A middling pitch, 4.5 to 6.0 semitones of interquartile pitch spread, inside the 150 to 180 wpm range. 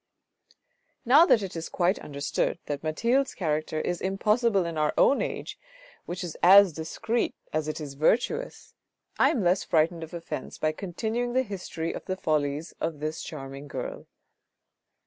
Yes: medium, 175 Hz; wide, 5.6 semitones; average, 160 wpm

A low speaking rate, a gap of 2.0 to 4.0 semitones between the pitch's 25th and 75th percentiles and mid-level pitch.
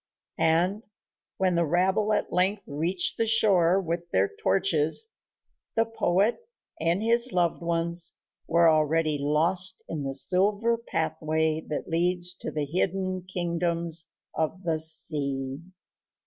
Yes: slow, 125 wpm; average, 3.1 semitones; medium, 170 Hz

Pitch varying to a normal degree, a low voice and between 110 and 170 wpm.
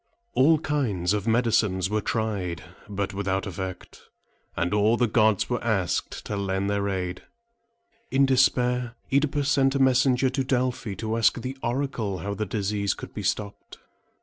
Yes: average, 4.4 semitones; low, 110 Hz; average, 155 wpm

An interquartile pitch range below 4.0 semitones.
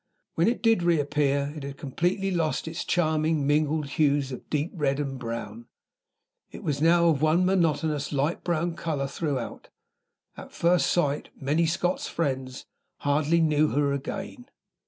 Yes: average, 3.2 semitones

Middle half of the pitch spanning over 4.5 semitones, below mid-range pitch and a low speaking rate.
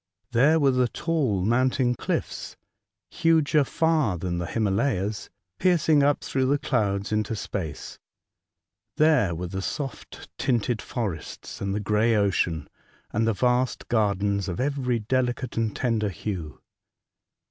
Yes: average, 5.0 semitones; low, 115 Hz; slow, 130 wpm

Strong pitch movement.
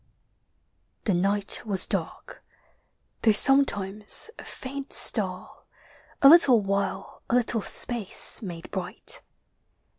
No: average, 4.1 semitones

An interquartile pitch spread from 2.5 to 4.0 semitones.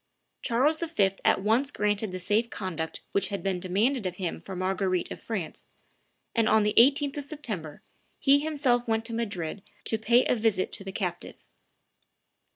No: average, 4.5 semitones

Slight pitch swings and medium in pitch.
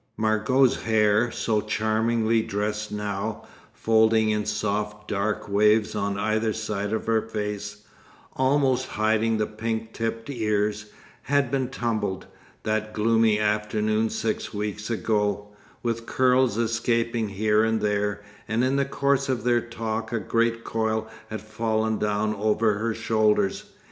No: narrow, 1.4 semitones; low, 110 Hz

